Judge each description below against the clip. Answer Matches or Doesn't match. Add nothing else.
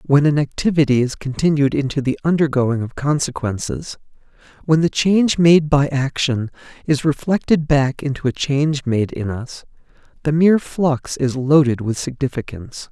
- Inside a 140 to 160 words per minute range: Matches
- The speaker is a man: Matches